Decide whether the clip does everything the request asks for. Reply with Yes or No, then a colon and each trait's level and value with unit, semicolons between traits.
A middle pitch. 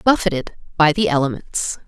Yes: medium, 165 Hz